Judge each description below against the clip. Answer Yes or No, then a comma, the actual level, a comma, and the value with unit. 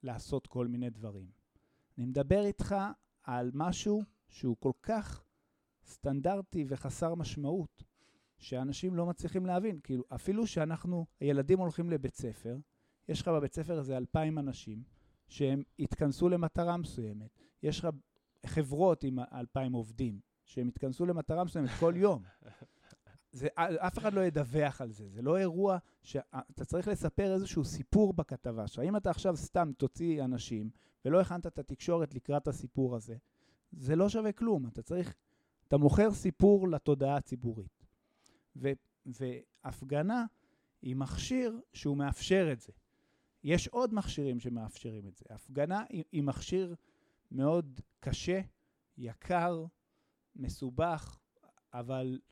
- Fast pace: No, average, 125 wpm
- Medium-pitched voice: Yes, medium, 145 Hz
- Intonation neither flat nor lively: No, wide, 5.8 semitones